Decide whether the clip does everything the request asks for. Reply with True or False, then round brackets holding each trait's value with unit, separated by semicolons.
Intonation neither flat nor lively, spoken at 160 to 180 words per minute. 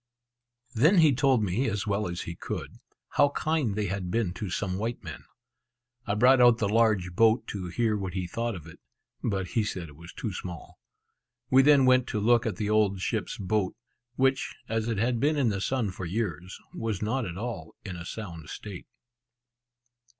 False (4.4 semitones; 195 wpm)